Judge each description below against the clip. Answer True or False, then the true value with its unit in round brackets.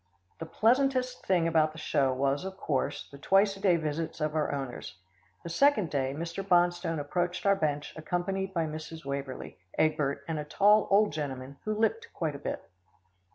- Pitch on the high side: False (165 Hz)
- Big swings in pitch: False (5.0 semitones)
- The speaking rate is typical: True (180 wpm)